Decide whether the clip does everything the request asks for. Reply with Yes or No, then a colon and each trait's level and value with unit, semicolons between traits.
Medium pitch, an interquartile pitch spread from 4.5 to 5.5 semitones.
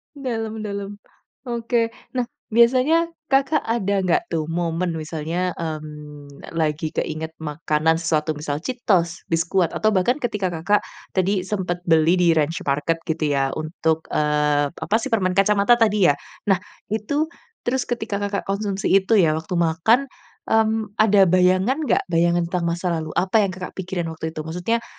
Yes: medium, 180 Hz; average, 5.0 semitones